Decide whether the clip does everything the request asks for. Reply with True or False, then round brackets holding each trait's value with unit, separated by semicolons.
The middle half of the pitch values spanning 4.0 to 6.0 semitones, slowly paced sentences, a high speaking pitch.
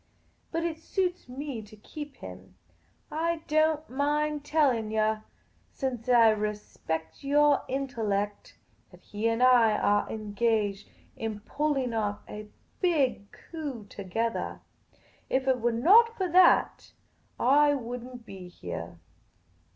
True (5.6 semitones; 130 wpm; 245 Hz)